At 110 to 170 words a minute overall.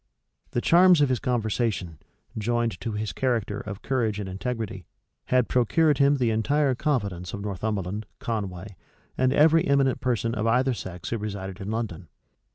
Yes: average, 160 wpm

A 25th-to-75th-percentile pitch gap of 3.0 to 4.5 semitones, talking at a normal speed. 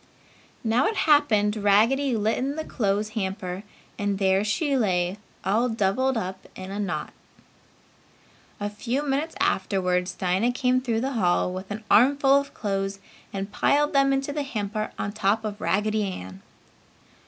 No: average, 5.1 semitones; average, 155 wpm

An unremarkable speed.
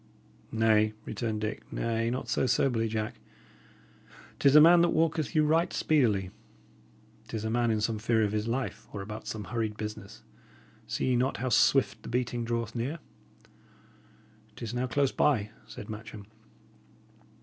Yes: average, 160 wpm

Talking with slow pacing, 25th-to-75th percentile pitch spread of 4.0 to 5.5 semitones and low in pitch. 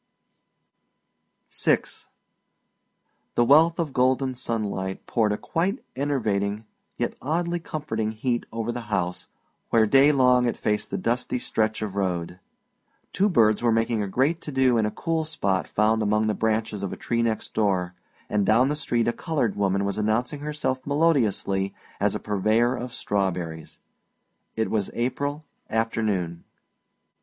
No: average, 150 wpm; average, 4.3 semitones; low, 115 Hz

